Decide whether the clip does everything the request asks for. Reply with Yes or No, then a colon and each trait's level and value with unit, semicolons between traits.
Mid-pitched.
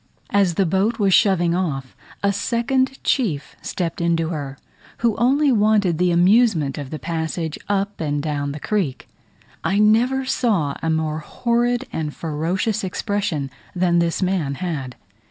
Yes: medium, 180 Hz